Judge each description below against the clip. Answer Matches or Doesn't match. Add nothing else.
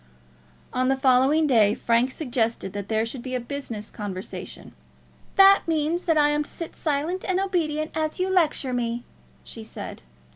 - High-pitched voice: Matches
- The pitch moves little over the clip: Doesn't match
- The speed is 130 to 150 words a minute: Doesn't match